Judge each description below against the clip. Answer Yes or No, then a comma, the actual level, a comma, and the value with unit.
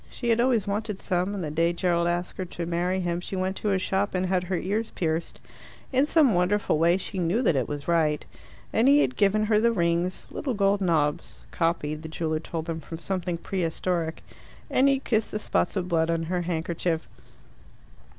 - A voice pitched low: No, medium, 180 Hz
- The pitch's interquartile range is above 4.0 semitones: No, average, 3.5 semitones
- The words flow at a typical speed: No, fast, 210 wpm